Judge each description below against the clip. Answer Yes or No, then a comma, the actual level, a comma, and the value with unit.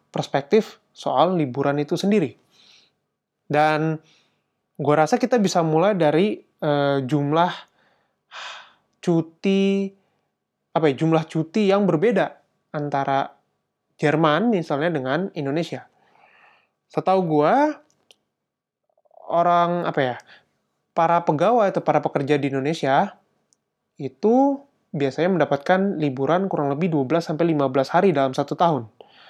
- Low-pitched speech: No, medium, 160 Hz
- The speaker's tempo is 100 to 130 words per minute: Yes, average, 105 wpm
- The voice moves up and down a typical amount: Yes, average, 4.2 semitones